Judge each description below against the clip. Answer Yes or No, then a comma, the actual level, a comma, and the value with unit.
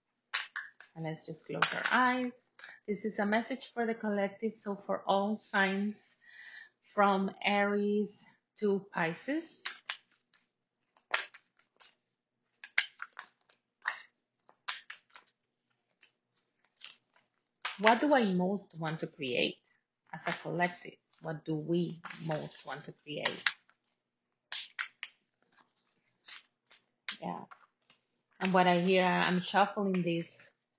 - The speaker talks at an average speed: No, slow, 90 wpm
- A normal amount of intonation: Yes, average, 4.0 semitones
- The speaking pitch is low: No, high, 195 Hz